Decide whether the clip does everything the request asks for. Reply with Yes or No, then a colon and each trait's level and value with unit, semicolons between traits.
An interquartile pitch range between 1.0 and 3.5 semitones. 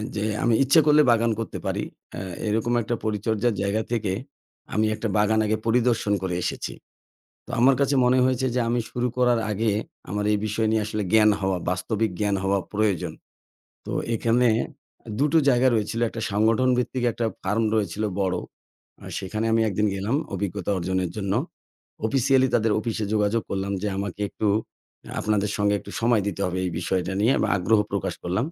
Yes: average, 2.7 semitones